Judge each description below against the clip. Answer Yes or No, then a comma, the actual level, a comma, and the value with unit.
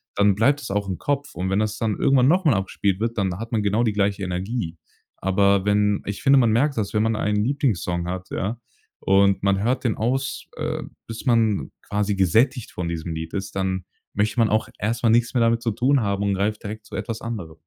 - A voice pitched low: Yes, low, 105 Hz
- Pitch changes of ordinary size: Yes, average, 3.0 semitones